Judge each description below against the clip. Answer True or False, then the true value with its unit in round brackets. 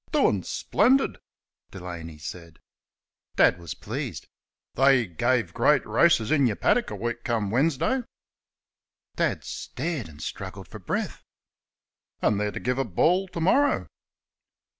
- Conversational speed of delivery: False (130 wpm)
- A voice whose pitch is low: True (120 Hz)